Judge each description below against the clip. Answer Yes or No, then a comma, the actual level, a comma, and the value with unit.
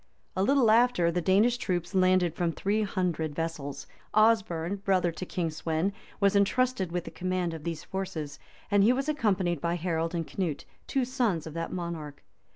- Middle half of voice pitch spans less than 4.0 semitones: Yes, average, 3.5 semitones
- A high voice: No, medium, 180 Hz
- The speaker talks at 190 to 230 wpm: No, average, 175 wpm